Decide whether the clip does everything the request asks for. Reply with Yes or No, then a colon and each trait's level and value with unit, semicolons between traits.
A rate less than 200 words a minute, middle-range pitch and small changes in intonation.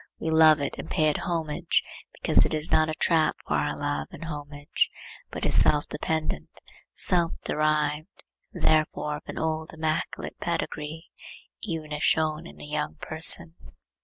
Yes: average, 160 wpm; medium, 155 Hz; narrow, 1.2 semitones